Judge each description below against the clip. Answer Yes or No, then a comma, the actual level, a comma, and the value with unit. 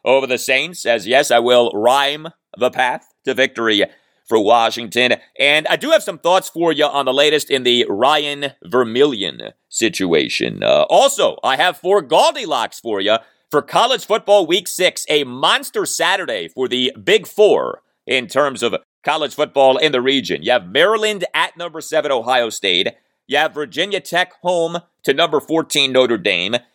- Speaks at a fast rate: No, average, 170 wpm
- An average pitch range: No, wide, 5.8 semitones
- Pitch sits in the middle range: Yes, medium, 150 Hz